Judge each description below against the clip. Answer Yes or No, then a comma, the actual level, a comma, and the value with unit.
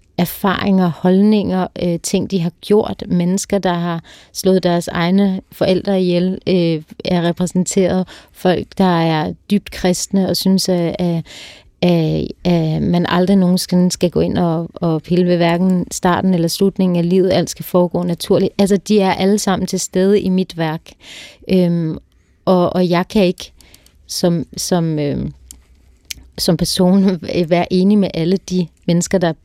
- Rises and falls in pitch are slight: Yes, narrow, 1.7 semitones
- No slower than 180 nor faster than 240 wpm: No, average, 160 wpm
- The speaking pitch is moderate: Yes, medium, 180 Hz